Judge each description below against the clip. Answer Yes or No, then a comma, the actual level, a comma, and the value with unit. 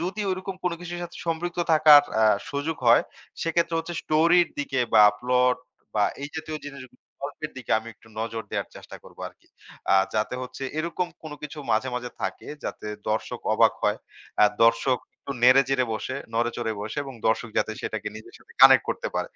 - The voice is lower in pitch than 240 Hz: Yes, low, 135 Hz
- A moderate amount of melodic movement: No, wide, 5.9 semitones